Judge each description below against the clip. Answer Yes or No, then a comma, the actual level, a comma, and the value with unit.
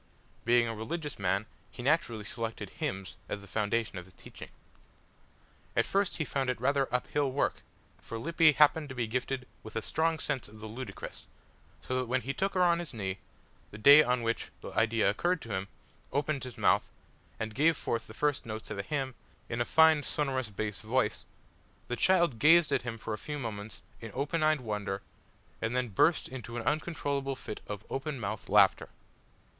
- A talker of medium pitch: No, low, 125 Hz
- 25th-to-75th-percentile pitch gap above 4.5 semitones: Yes, average, 5.1 semitones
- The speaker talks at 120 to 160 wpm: No, average, 195 wpm